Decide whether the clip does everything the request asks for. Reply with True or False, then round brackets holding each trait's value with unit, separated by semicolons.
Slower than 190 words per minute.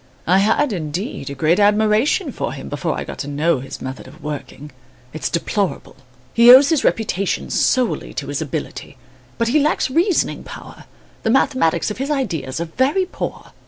True (175 wpm)